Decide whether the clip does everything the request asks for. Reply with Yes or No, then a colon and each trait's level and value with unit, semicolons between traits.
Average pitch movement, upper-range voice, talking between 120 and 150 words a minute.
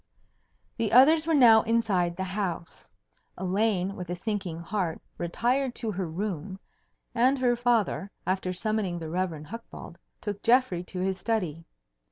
Yes: average, 4.5 semitones; high, 195 Hz; average, 145 wpm